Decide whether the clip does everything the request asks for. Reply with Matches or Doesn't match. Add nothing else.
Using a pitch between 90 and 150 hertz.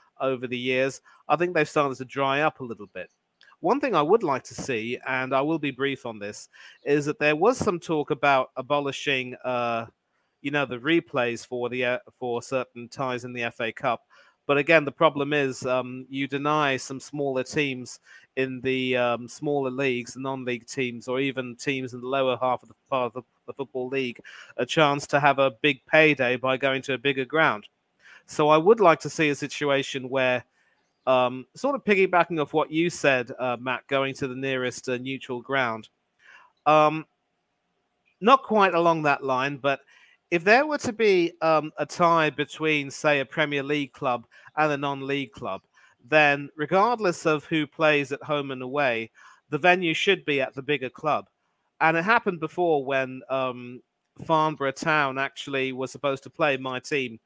Matches